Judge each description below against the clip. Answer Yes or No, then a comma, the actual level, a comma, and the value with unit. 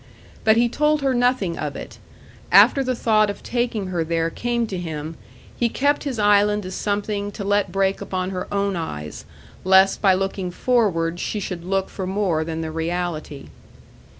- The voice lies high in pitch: Yes, high, 195 Hz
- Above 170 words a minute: Yes, average, 180 wpm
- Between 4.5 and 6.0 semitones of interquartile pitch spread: No, average, 3.8 semitones